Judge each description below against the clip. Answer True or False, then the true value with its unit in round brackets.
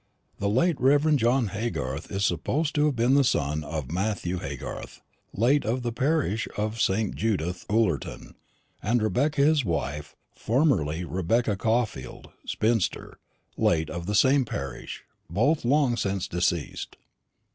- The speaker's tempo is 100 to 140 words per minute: True (135 wpm)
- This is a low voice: True (110 Hz)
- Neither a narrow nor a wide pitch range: False (6.8 semitones)